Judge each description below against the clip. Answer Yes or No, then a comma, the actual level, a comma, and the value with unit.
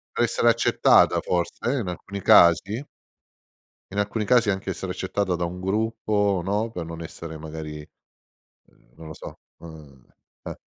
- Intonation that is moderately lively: Yes, average, 4.4 semitones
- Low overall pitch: Yes, very low, 95 Hz